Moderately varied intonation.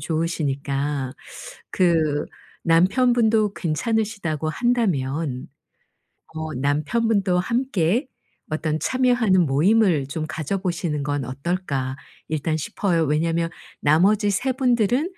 No: wide, 6.2 semitones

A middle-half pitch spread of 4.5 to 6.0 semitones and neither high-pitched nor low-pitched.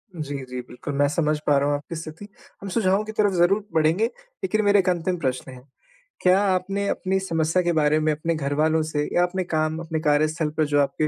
No: average, 3.6 semitones; medium, 160 Hz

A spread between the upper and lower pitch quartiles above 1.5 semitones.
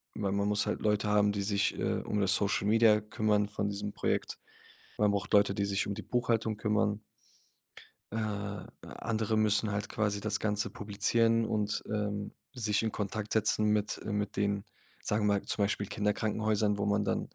No: narrow, 1.1 semitones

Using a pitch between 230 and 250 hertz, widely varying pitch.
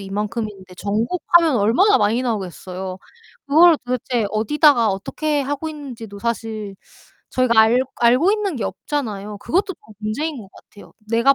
Yes: high, 235 Hz; wide, 5.9 semitones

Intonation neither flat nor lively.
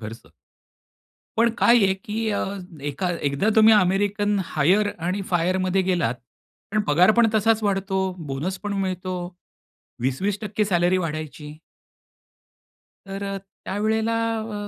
Yes: average, 3.2 semitones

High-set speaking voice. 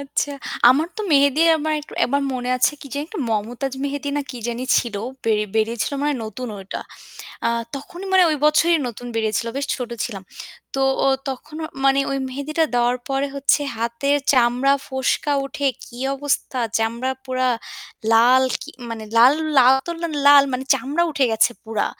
Yes: very high, 265 Hz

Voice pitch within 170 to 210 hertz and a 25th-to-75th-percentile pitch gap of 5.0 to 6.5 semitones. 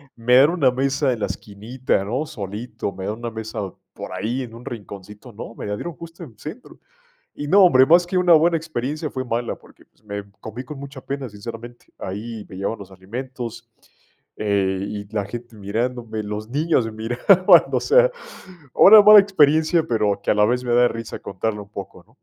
No: low, 120 Hz; average, 5.3 semitones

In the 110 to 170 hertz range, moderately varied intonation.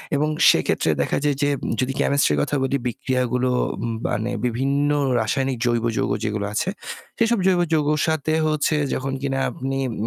Yes: low, 135 Hz; average, 3.2 semitones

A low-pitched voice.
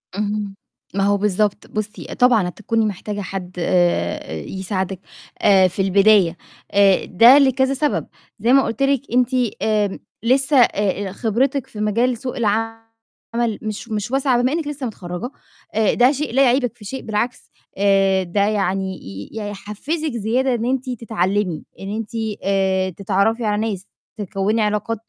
No: high, 215 Hz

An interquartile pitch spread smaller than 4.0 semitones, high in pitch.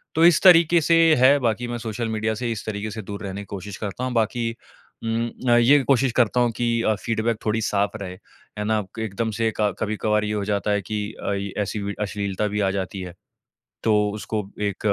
No: narrow, 2.5 semitones; low, 110 Hz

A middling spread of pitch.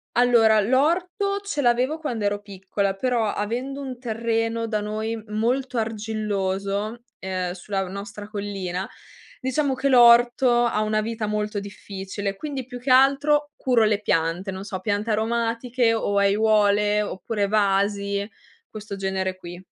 Yes: average, 3.2 semitones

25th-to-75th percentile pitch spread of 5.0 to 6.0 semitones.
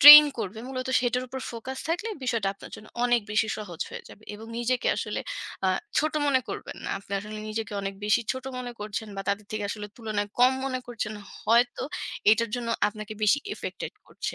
No: average, 3.2 semitones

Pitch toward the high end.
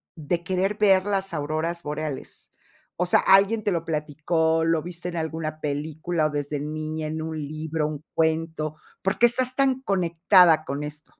No: medium, 160 Hz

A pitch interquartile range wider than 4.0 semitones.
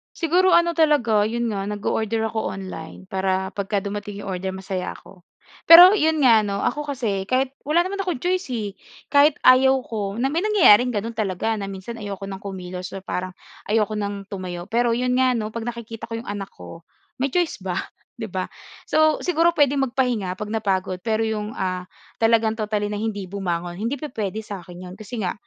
Yes: average, 4.6 semitones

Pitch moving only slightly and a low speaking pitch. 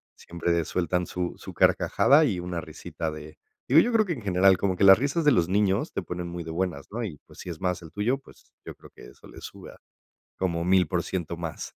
No: average, 3.2 semitones; very low, 90 Hz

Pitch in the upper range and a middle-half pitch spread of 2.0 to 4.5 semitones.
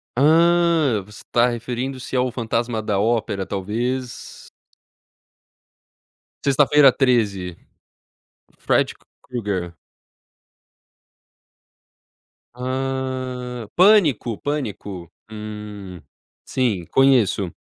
No: low, 120 Hz; average, 4.0 semitones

